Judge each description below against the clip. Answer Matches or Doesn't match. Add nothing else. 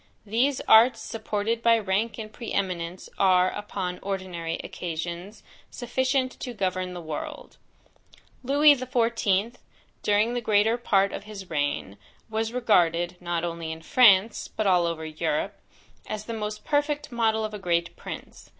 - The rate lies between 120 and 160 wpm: Matches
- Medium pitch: Doesn't match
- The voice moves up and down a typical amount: Matches